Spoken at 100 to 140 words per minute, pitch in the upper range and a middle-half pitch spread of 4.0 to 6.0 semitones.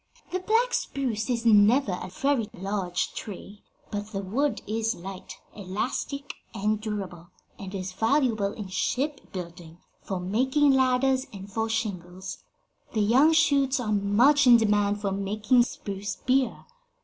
Yes: slow, 135 wpm; high, 215 Hz; average, 4.8 semitones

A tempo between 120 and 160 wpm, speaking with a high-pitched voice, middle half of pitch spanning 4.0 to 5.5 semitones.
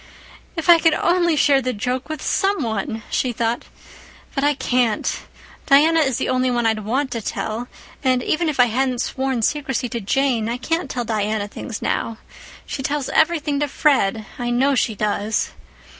No: average, 175 wpm; very high, 255 Hz; average, 4.3 semitones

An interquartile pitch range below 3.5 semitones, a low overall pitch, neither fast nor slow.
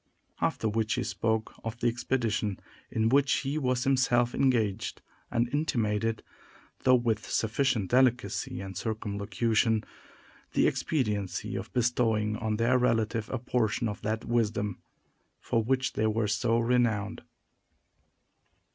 No: narrow, 2.5 semitones; low, 115 Hz; slow, 125 wpm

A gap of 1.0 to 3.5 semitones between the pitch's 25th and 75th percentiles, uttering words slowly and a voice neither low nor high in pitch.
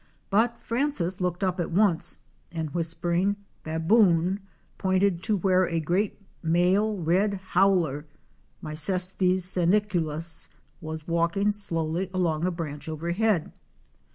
Yes: average, 3.0 semitones; slow, 110 wpm; medium, 180 Hz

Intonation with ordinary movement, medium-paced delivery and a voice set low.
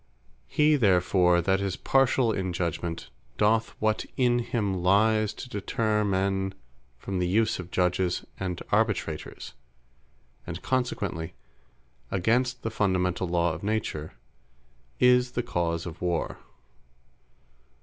No: average, 4.0 semitones; slow, 120 wpm; very low, 95 Hz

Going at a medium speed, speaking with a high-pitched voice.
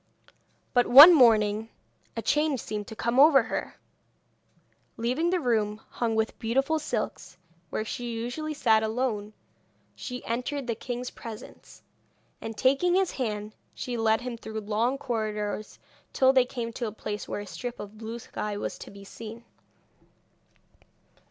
Yes: average, 150 wpm; high, 230 Hz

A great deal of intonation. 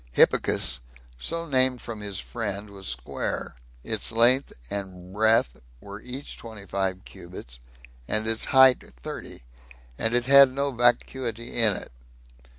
No: average, 4.5 semitones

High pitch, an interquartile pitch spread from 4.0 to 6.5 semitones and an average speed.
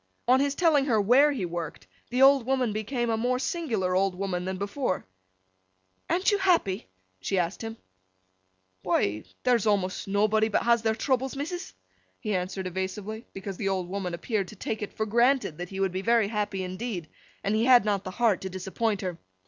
Yes: high, 210 Hz; average, 4.6 semitones; average, 190 wpm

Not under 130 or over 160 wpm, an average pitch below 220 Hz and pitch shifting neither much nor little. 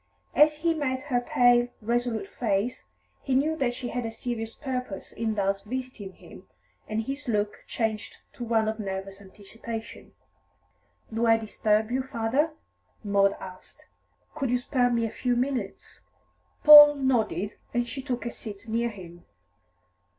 No: average, 150 wpm; high, 235 Hz; average, 3.3 semitones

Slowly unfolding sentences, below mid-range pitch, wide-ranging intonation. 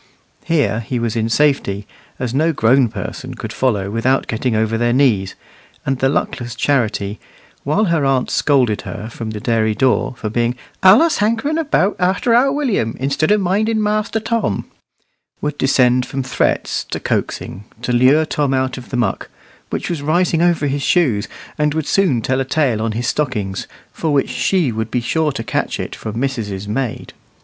No: average, 180 wpm; low, 130 Hz; wide, 5.8 semitones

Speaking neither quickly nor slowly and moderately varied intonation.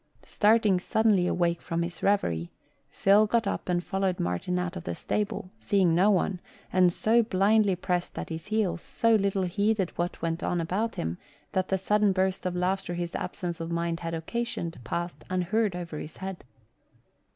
Yes: average, 175 wpm; average, 3.0 semitones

